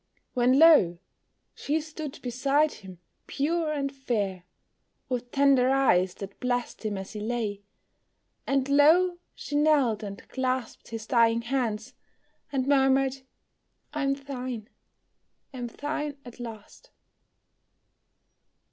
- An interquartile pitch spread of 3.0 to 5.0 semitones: Yes, average, 3.7 semitones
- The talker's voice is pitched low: No, very high, 260 Hz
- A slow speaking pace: Yes, slow, 115 wpm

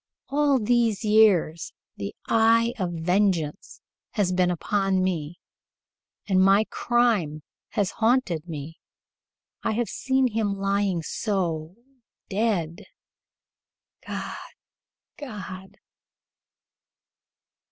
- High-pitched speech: Yes, high, 195 Hz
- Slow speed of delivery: Yes, slow, 90 wpm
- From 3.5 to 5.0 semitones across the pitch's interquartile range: Yes, average, 4.3 semitones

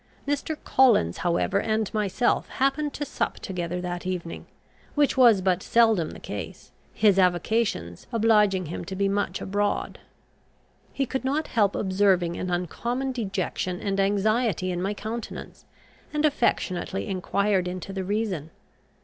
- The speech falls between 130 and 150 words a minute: Yes, average, 140 wpm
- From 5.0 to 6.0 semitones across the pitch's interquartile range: No, average, 4.0 semitones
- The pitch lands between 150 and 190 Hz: No, high, 200 Hz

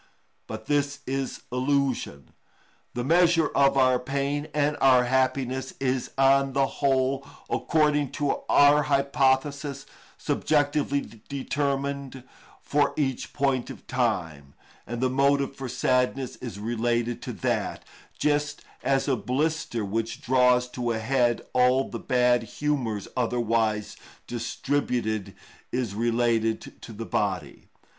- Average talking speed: No, slow, 120 wpm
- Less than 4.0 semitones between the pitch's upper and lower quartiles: Yes, average, 2.9 semitones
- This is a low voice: Yes, low, 130 Hz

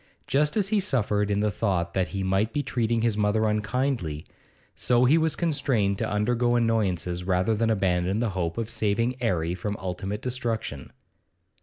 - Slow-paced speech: No, average, 170 wpm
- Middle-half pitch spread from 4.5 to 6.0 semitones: No, average, 3.9 semitones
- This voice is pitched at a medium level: No, low, 105 Hz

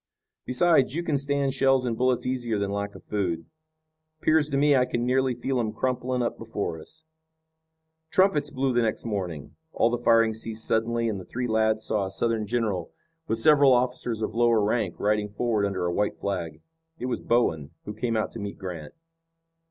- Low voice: Yes, low, 115 Hz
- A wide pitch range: No, average, 3.7 semitones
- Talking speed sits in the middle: Yes, average, 190 wpm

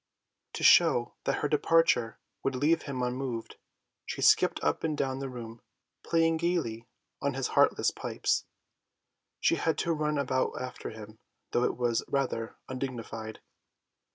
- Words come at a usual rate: Yes, average, 145 wpm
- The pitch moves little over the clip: No, average, 4.1 semitones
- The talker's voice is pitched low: Yes, low, 130 Hz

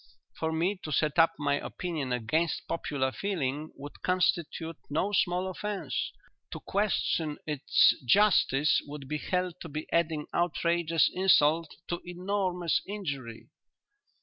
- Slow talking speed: Yes, slow, 125 wpm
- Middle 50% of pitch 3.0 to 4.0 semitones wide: Yes, average, 3.5 semitones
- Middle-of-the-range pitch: Yes, medium, 165 Hz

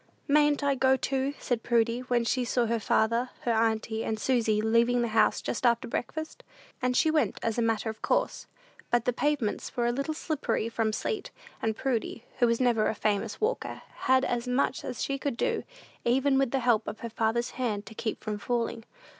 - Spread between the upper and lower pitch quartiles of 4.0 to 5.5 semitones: No, average, 2.8 semitones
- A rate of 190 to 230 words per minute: Yes, fast, 205 wpm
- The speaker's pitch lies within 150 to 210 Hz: No, high, 240 Hz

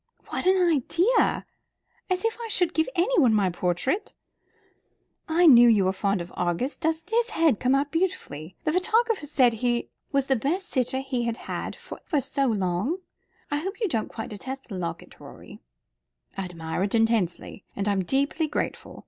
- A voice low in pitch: No, very high, 265 Hz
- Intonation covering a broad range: Yes, wide, 8.7 semitones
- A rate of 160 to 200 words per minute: Yes, average, 175 wpm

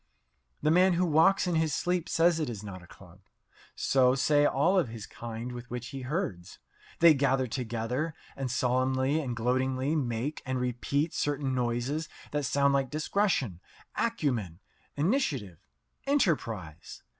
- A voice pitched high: No, low, 135 Hz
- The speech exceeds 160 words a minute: No, average, 145 wpm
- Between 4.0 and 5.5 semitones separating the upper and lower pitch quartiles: Yes, average, 4.5 semitones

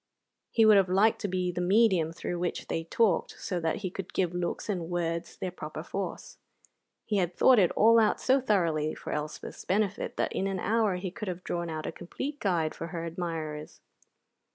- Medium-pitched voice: Yes, medium, 180 Hz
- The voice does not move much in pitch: No, average, 3.4 semitones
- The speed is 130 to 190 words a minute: No, average, 200 wpm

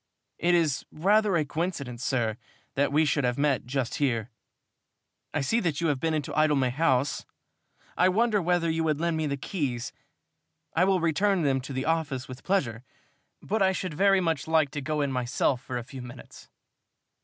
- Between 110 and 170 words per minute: No, average, 190 wpm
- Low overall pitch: No, medium, 150 Hz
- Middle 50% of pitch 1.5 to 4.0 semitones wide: No, average, 4.4 semitones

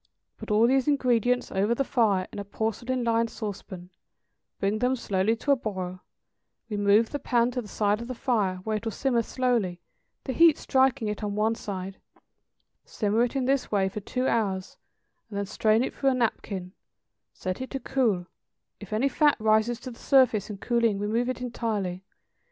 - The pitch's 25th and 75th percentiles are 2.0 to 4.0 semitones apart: Yes, average, 3.7 semitones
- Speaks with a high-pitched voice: Yes, high, 225 Hz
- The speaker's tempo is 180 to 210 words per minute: Yes, average, 190 wpm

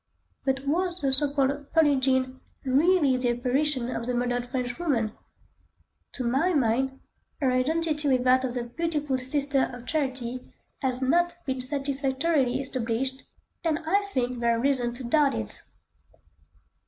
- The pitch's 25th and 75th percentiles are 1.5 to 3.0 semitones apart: Yes, average, 2.7 semitones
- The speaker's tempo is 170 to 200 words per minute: No, average, 150 wpm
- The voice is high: Yes, very high, 265 Hz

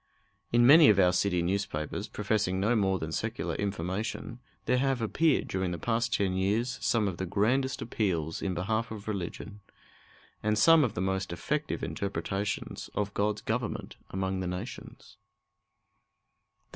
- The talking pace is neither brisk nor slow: Yes, average, 150 wpm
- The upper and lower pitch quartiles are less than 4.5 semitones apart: Yes, average, 3.5 semitones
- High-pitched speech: No, low, 100 Hz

